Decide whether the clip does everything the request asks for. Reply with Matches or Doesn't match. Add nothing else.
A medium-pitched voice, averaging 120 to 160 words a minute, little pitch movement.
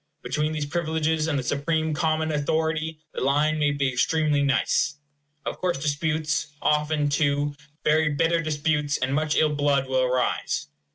Matches